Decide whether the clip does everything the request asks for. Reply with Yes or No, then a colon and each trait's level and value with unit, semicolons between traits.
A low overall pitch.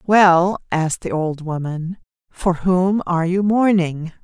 No: medium, 175 Hz